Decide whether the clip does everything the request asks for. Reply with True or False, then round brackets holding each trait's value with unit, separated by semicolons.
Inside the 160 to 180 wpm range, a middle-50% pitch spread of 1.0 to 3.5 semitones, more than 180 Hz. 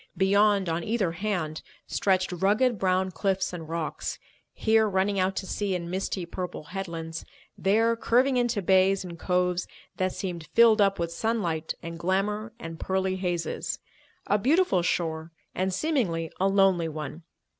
False (150 wpm; 3.2 semitones; 190 Hz)